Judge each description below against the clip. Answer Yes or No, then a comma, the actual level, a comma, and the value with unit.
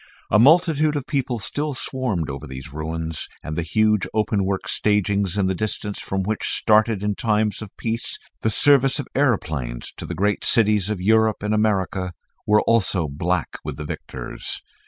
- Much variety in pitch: No, average, 3.8 semitones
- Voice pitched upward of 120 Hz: No, low, 105 Hz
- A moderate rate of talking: Yes, average, 175 wpm